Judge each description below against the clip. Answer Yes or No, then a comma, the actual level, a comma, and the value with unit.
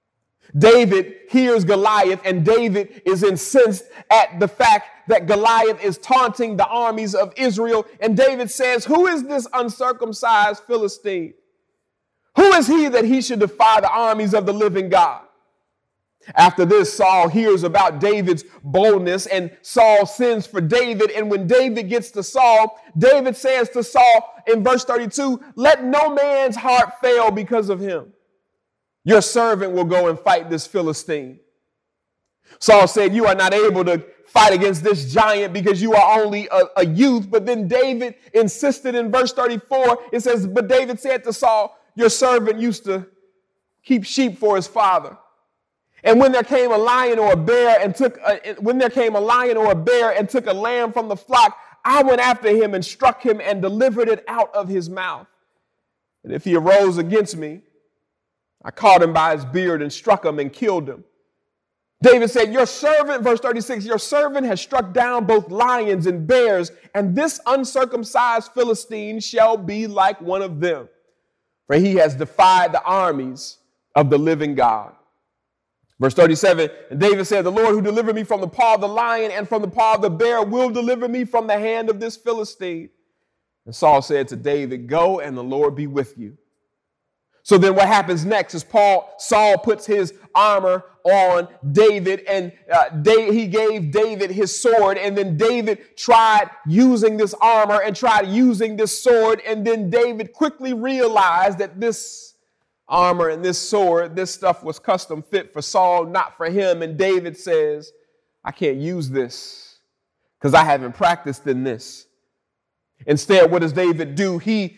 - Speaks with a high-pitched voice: Yes, high, 215 Hz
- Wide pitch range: No, average, 4.6 semitones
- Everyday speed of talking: Yes, average, 175 wpm